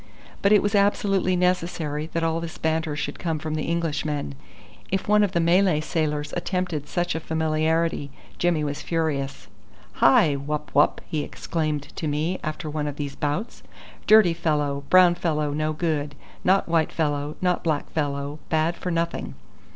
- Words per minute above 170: No, average, 165 wpm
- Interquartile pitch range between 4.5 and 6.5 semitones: No, average, 2.7 semitones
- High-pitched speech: No, medium, 160 Hz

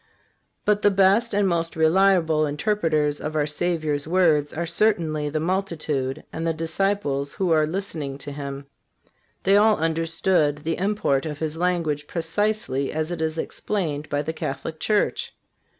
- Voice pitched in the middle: Yes, medium, 160 Hz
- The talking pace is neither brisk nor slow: Yes, average, 155 wpm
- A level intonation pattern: No, average, 4.1 semitones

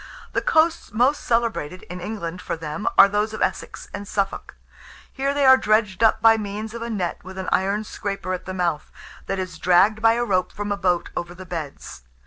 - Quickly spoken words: Yes, fast, 210 wpm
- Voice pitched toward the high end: Yes, high, 200 Hz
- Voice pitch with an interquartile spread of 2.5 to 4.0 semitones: Yes, average, 3.5 semitones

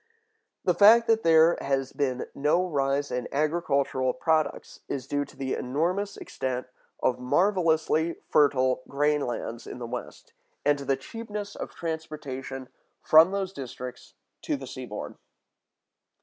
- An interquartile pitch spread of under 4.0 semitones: No, average, 4.4 semitones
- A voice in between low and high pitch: Yes, medium, 145 Hz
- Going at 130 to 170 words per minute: Yes, slow, 135 wpm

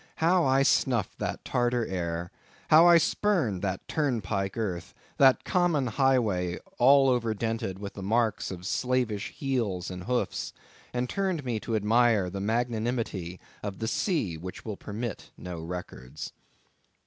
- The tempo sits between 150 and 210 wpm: No, slow, 135 wpm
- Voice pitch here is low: Yes, low, 115 Hz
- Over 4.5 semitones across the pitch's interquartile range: Yes, average, 5.2 semitones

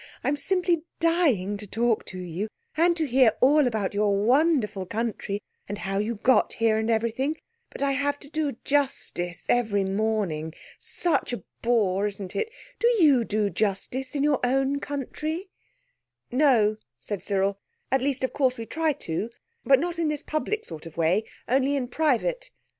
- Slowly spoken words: No, average, 170 wpm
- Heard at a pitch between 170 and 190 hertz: No, high, 245 Hz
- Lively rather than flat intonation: Yes, wide, 5.9 semitones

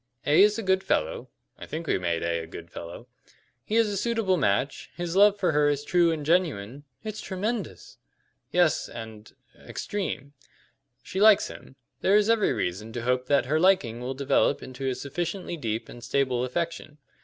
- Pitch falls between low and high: Yes, medium, 150 Hz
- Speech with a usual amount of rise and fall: No, wide, 7.4 semitones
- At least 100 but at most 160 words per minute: No, average, 190 wpm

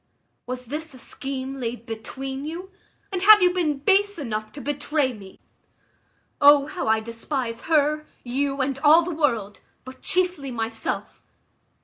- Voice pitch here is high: Yes, very high, 275 Hz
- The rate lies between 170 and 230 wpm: No, average, 145 wpm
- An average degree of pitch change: Yes, average, 4.5 semitones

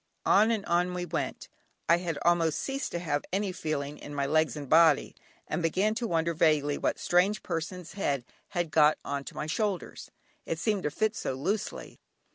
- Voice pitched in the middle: Yes, medium, 170 Hz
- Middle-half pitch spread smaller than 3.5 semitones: No, average, 3.9 semitones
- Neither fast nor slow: Yes, average, 190 wpm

